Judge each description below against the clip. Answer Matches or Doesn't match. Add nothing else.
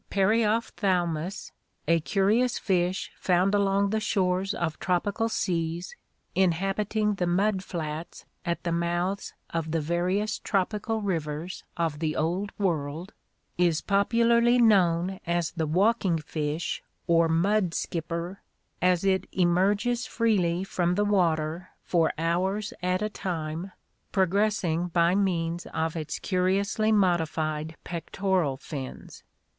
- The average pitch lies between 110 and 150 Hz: Doesn't match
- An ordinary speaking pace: Doesn't match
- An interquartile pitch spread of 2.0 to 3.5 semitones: Matches